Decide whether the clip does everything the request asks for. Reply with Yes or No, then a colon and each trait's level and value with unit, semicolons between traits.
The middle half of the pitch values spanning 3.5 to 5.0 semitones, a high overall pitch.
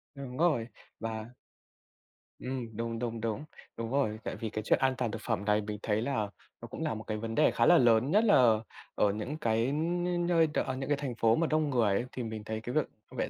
No: average, 4.2 semitones; low, 115 Hz